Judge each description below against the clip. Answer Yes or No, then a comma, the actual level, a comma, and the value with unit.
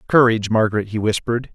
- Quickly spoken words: No, average, 155 wpm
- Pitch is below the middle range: Yes, low, 110 Hz